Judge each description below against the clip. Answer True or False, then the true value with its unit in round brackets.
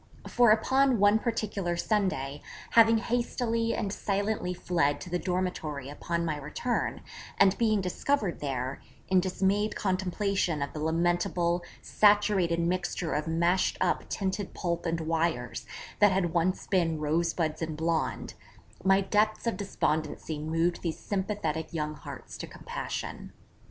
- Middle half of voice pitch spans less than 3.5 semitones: False (4.0 semitones)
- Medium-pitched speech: True (180 Hz)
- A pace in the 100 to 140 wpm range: True (135 wpm)